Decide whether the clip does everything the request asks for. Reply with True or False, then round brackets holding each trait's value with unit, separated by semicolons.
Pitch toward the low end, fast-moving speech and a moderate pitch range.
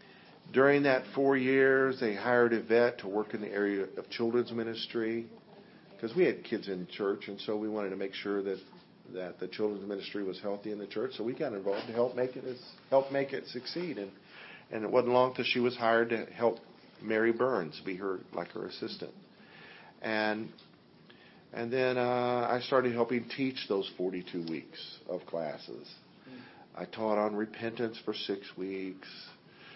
False (115 Hz; 180 wpm; 3.4 semitones)